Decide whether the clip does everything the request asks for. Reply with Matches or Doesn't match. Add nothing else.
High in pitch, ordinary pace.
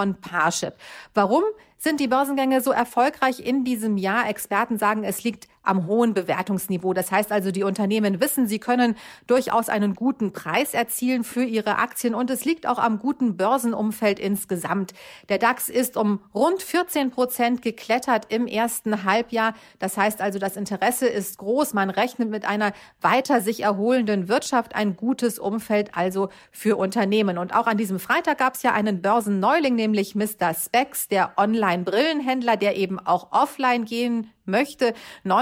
Matches